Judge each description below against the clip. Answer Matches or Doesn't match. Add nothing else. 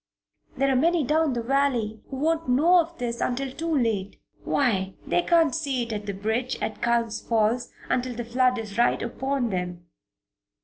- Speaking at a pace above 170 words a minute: Matches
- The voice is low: Doesn't match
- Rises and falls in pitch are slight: Doesn't match